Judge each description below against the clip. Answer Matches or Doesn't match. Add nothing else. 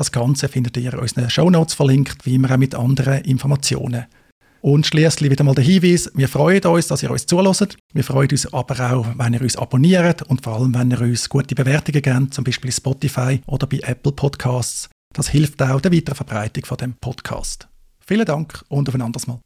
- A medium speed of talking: Doesn't match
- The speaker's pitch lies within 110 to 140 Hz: Matches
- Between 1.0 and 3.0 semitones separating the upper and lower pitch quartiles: Matches